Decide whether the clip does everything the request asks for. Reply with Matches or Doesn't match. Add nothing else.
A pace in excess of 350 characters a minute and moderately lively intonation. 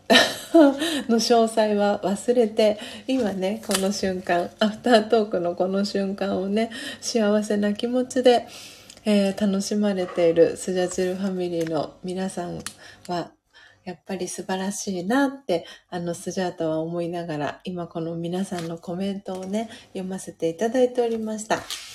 Doesn't match